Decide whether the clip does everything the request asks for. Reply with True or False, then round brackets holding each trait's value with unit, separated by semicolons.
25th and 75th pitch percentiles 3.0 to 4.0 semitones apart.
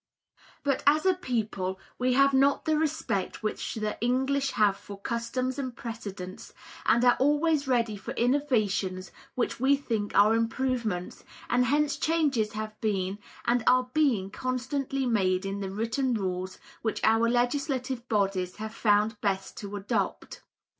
False (4.5 semitones)